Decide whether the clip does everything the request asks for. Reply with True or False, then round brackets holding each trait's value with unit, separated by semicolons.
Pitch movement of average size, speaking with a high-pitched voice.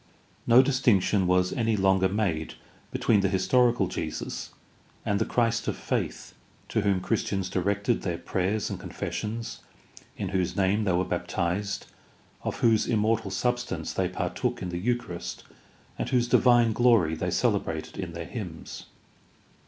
False (4.0 semitones; 100 Hz)